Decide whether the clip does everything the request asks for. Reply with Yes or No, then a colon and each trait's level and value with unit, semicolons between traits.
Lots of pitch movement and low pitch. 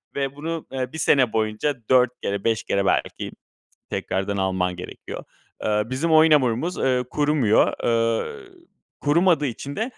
Yes: wide, 5.8 semitones; low, 130 Hz